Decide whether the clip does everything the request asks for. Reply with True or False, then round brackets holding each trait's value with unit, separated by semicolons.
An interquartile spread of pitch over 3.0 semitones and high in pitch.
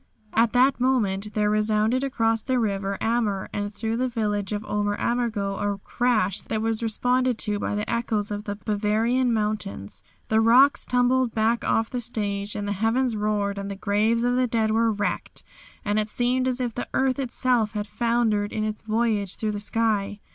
False (2.6 semitones; 220 Hz)